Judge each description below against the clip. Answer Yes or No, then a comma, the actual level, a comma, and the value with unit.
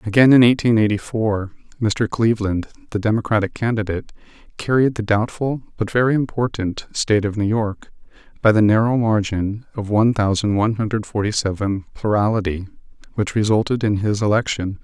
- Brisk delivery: No, average, 150 wpm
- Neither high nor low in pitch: No, low, 110 Hz